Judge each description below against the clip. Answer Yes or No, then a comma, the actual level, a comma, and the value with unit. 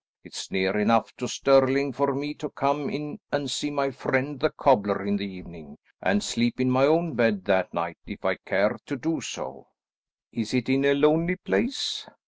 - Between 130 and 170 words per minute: No, average, 190 wpm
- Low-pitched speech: Yes, low, 130 Hz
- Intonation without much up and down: No, wide, 5.6 semitones